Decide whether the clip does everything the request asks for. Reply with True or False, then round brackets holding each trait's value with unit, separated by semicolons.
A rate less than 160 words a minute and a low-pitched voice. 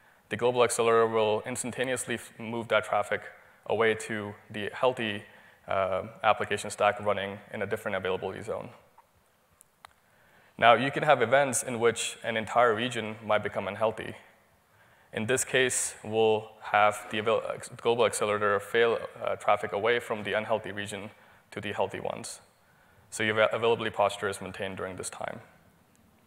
True (145 wpm; 115 Hz)